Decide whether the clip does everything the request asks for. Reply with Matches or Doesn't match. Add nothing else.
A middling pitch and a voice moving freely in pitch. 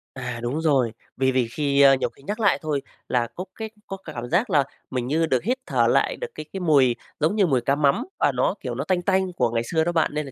Matches